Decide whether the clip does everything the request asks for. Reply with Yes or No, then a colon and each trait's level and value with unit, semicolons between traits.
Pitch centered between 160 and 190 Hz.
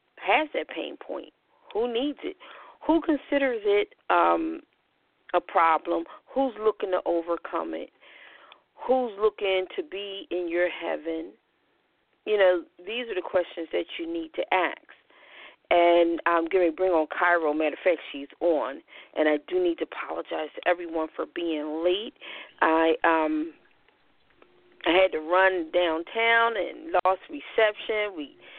Yes: medium, 185 Hz